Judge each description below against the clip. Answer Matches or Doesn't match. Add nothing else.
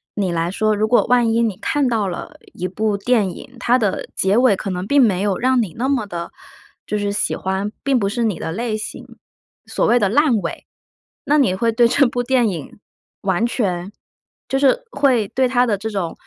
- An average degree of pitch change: Matches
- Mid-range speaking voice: Doesn't match